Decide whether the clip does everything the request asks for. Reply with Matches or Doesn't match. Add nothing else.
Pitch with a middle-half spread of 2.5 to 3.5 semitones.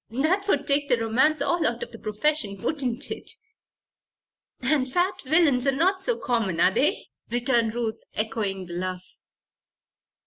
Doesn't match